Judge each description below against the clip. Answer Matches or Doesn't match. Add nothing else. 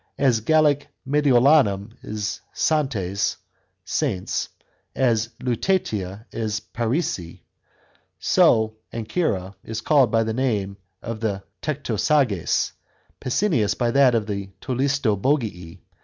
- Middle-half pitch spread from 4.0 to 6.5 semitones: Matches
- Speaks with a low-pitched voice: Matches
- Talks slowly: Matches